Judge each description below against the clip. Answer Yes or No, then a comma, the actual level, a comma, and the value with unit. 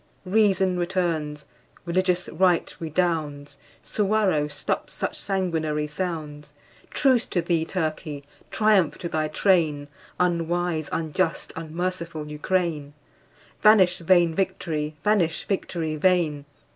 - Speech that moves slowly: Yes, slow, 100 wpm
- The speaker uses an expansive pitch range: No, average, 3.2 semitones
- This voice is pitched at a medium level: Yes, medium, 170 Hz